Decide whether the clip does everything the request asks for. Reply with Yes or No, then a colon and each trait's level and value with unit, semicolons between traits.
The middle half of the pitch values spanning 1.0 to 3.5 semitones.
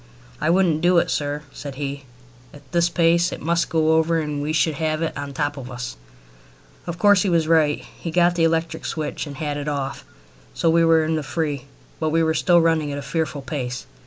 Yes: narrow, 2.5 semitones